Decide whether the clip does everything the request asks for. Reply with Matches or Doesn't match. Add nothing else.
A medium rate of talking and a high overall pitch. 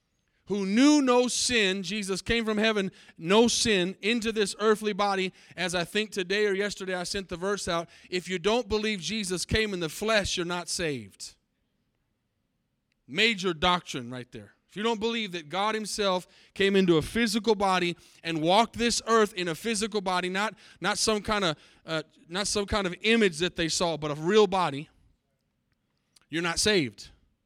Matches